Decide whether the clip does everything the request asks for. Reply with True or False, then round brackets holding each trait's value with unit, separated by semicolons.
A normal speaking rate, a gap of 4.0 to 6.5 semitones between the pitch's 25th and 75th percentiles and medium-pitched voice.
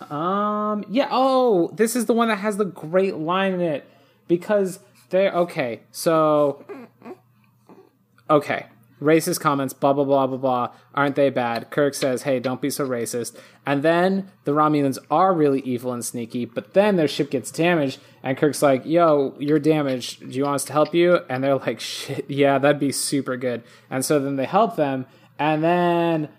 True (185 wpm; 4.5 semitones; 145 Hz)